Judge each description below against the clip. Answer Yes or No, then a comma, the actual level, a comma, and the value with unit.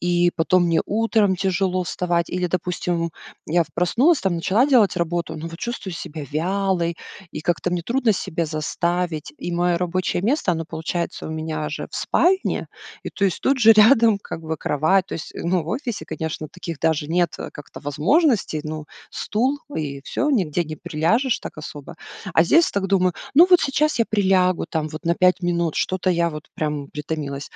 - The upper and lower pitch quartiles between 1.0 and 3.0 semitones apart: No, average, 3.7 semitones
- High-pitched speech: No, medium, 175 Hz